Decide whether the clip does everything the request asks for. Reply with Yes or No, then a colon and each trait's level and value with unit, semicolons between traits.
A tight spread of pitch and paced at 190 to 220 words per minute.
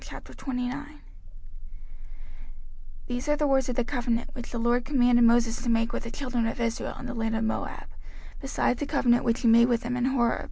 Yes: narrow, 1.8 semitones; average, 200 wpm